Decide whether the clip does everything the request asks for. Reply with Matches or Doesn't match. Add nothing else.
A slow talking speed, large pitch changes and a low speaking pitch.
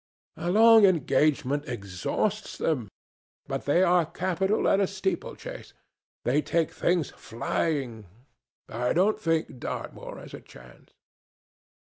Doesn't match